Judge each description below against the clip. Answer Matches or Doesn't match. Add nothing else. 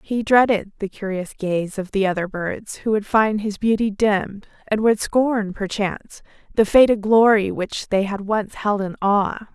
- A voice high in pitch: Matches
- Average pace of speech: Matches